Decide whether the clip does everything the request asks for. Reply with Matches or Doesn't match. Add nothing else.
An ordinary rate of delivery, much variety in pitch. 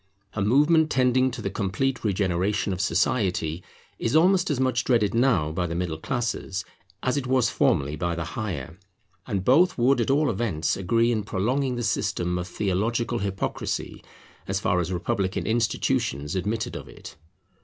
Matches